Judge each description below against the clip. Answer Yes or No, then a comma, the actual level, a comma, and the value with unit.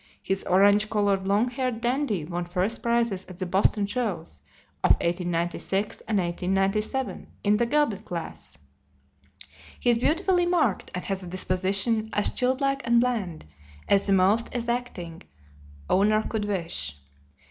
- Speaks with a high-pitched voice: Yes, high, 205 Hz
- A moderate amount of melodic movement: Yes, average, 4.4 semitones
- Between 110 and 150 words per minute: Yes, slow, 135 wpm